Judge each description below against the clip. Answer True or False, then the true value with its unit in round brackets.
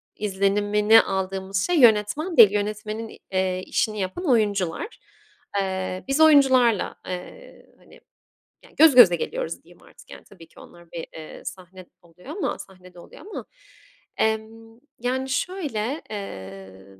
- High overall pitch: True (210 Hz)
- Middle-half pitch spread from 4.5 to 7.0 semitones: True (4.9 semitones)